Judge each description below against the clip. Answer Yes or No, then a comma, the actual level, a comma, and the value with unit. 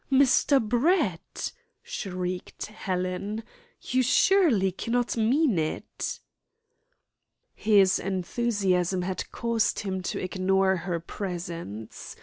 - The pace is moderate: No, slow, 90 wpm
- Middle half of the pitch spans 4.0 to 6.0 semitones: Yes, average, 4.4 semitones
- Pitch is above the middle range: Yes, high, 195 Hz